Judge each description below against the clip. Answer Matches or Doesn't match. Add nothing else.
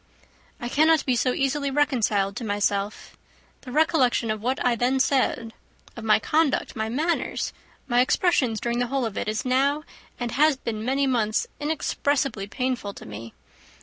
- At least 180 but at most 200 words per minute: Doesn't match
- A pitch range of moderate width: Matches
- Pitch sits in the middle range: Doesn't match